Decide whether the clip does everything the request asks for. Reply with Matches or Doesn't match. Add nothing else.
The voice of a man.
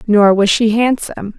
Doesn't match